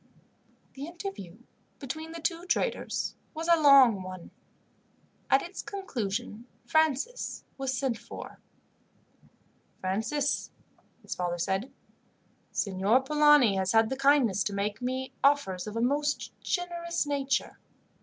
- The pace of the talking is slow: Yes, slow, 120 wpm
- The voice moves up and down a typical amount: No, wide, 6.3 semitones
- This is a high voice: Yes, very high, 265 Hz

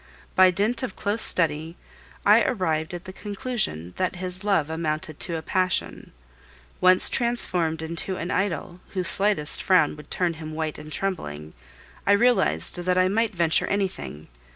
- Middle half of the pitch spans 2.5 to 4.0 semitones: Yes, average, 3.6 semitones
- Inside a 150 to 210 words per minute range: Yes, average, 155 wpm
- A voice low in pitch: No, medium, 180 Hz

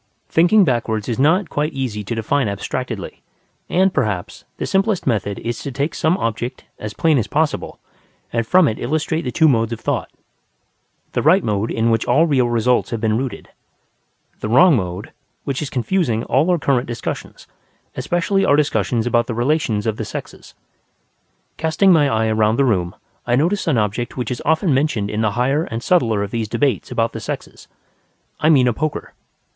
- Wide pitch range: Yes, wide, 5.7 semitones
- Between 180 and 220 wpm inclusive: Yes, average, 185 wpm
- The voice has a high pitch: No, low, 125 Hz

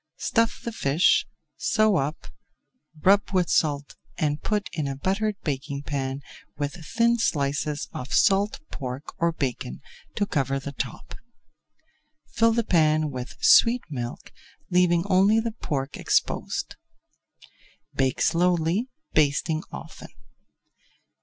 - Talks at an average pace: No, slow, 120 wpm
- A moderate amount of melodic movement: No, wide, 6.2 semitones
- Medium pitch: Yes, medium, 155 Hz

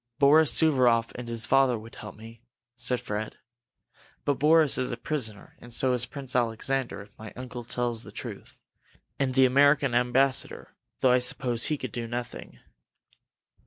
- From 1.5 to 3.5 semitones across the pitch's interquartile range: Yes, narrow, 2.6 semitones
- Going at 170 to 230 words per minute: No, average, 160 wpm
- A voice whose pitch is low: Yes, low, 125 Hz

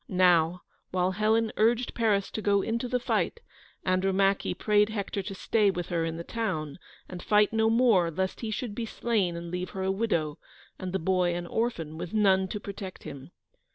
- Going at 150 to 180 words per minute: No, average, 190 wpm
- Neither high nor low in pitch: No, high, 195 Hz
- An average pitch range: Yes, average, 3.5 semitones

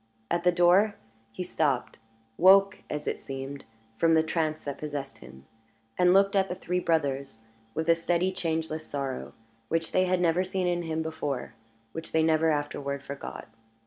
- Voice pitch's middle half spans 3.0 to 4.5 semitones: Yes, average, 3.9 semitones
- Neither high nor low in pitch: Yes, medium, 160 Hz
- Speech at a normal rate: Yes, average, 170 wpm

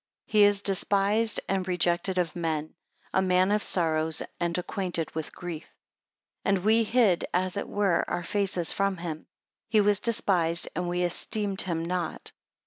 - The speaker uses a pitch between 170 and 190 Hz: Yes, medium, 185 Hz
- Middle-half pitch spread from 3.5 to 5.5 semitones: No, average, 2.8 semitones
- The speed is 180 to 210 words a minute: No, average, 165 wpm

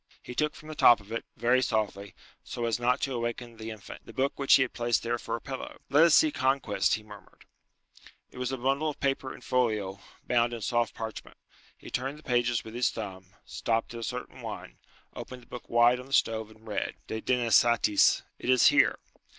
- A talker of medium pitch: No, low, 120 Hz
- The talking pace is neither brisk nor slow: No, fast, 215 wpm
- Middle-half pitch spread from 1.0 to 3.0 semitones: Yes, narrow, 2.5 semitones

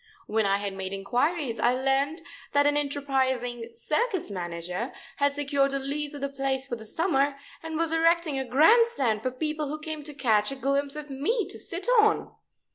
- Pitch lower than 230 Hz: No, very high, 275 Hz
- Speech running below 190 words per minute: No, average, 195 wpm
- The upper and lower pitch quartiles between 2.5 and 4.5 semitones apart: Yes, average, 3.6 semitones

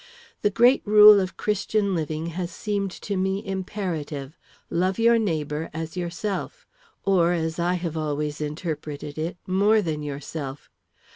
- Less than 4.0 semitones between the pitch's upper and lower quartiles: No, average, 4.3 semitones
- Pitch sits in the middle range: Yes, medium, 175 Hz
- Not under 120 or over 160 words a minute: Yes, average, 140 wpm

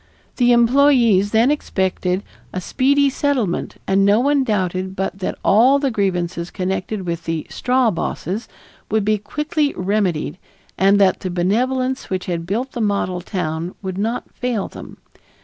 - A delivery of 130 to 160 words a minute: Yes, average, 150 wpm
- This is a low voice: No, high, 200 Hz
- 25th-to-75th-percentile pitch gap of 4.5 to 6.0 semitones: Yes, average, 5.2 semitones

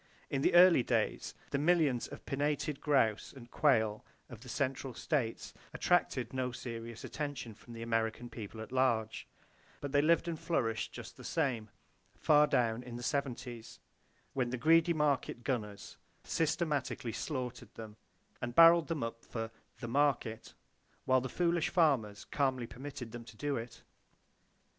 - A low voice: Yes, low, 130 Hz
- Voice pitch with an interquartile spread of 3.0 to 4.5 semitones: Yes, average, 4.0 semitones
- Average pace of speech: Yes, average, 155 wpm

